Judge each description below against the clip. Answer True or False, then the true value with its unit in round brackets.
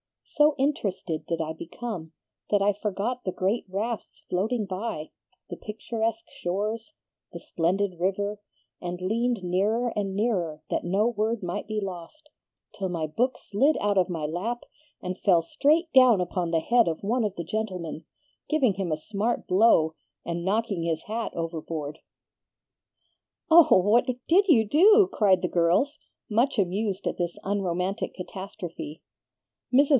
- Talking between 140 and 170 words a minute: True (150 wpm)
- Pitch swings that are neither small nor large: True (4.7 semitones)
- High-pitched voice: True (200 Hz)